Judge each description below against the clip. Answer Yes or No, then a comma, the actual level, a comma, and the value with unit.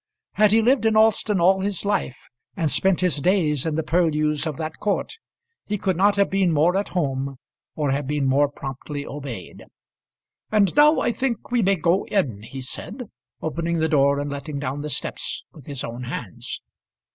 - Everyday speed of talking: Yes, average, 190 wpm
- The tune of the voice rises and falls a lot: Yes, wide, 5.7 semitones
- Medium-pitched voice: Yes, medium, 160 Hz